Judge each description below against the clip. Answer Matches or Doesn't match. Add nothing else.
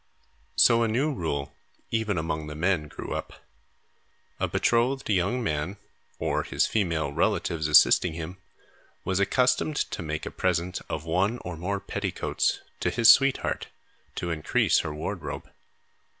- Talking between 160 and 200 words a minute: Doesn't match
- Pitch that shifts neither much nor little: Doesn't match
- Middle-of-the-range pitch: Doesn't match